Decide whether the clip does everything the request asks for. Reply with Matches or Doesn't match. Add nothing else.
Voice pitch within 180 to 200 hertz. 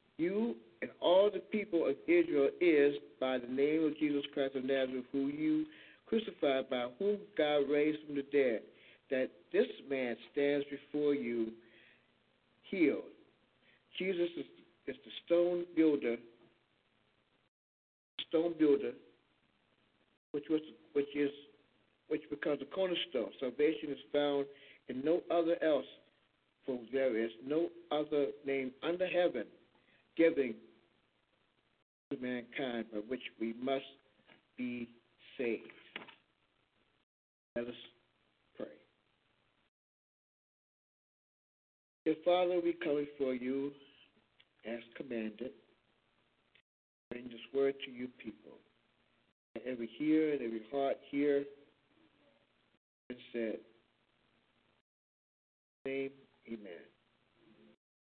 Doesn't match